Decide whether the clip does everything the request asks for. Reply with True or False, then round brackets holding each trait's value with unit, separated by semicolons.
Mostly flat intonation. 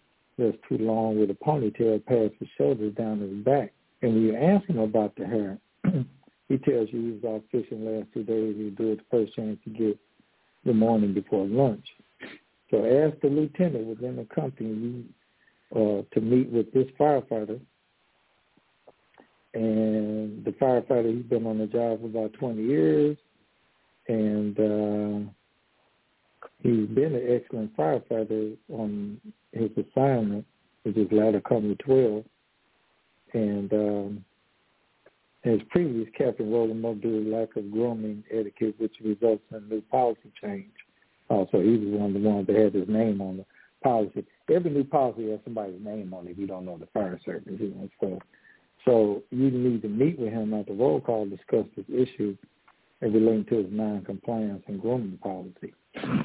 True (2.3 semitones)